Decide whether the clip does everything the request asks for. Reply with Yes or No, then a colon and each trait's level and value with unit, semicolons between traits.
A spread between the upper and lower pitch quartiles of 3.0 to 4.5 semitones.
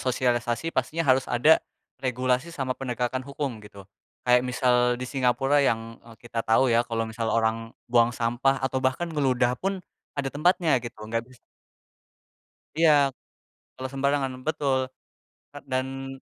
No: narrow, 2.5 semitones